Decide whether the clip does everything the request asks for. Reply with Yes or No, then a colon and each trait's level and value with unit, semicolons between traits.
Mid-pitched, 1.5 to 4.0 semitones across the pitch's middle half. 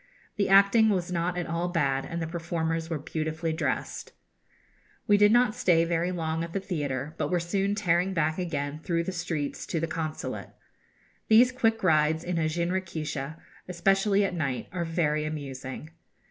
Yes: medium, 170 Hz; average, 3.0 semitones